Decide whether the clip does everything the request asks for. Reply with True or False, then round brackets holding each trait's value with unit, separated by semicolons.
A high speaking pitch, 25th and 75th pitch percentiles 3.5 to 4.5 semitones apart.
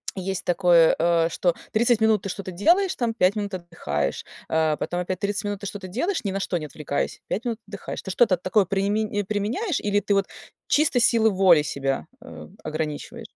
True (195 Hz; 3.8 semitones)